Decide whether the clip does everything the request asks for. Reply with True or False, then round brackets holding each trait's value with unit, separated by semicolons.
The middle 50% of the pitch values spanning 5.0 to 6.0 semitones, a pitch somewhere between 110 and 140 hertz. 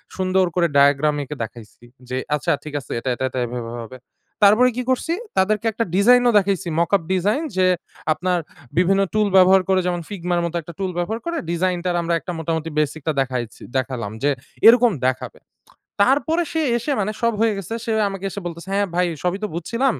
False (5.6 semitones; 185 Hz)